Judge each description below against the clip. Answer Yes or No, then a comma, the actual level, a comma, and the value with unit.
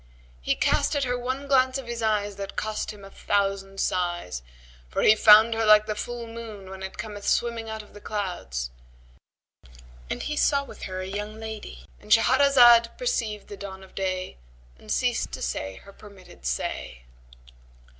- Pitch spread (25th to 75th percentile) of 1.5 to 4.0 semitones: Yes, average, 3.3 semitones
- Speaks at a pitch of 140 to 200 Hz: No, high, 210 Hz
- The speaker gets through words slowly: No, average, 170 wpm